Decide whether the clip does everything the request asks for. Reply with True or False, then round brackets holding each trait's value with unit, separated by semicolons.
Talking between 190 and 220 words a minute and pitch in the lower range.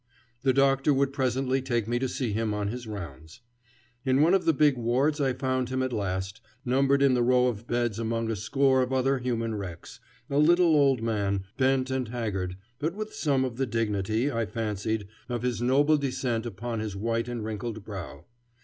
True (195 wpm; 120 Hz)